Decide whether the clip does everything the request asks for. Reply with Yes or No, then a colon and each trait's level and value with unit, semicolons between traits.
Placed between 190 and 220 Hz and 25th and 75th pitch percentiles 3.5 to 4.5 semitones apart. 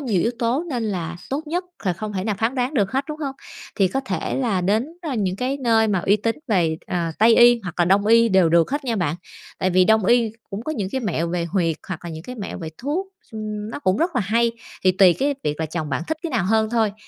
No: high, 215 Hz; average, 5.1 semitones